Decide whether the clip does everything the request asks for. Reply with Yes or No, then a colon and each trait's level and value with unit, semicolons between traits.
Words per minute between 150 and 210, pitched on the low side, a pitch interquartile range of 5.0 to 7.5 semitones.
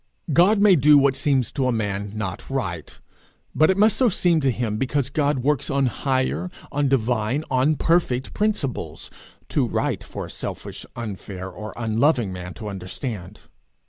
Yes: average, 165 wpm; low, 130 Hz; wide, 5.6 semitones